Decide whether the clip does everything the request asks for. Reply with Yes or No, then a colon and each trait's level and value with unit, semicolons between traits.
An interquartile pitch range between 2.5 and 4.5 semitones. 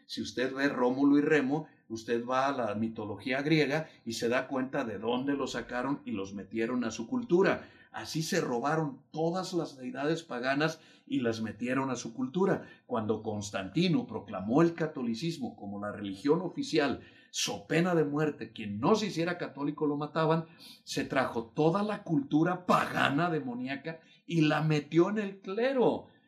No: average, 5.1 semitones